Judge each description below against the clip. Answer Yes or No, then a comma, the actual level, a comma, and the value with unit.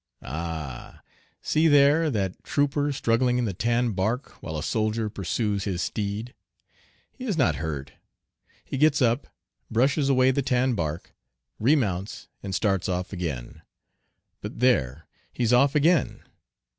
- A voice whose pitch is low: Yes, low, 115 Hz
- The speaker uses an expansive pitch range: Yes, wide, 6.7 semitones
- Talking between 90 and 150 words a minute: Yes, slow, 135 wpm